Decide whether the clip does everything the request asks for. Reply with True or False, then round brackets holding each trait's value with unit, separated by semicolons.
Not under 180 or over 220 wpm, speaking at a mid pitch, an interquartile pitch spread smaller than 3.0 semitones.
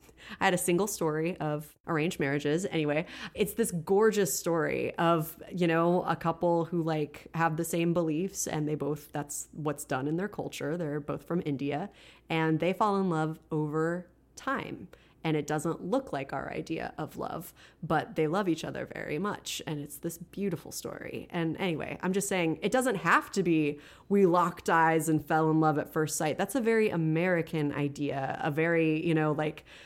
True (190 wpm; 165 Hz; 2.5 semitones)